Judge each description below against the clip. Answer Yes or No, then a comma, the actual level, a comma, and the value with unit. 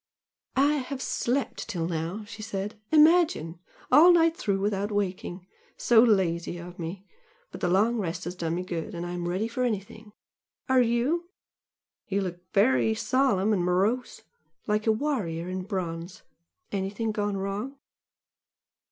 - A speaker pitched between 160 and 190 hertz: No, high, 205 Hz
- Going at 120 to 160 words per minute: Yes, average, 145 wpm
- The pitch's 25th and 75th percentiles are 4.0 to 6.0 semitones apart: Yes, average, 4.9 semitones